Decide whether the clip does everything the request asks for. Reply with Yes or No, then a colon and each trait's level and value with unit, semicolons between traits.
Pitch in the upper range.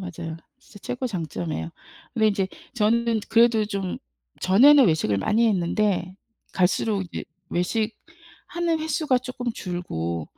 Yes: high, 210 Hz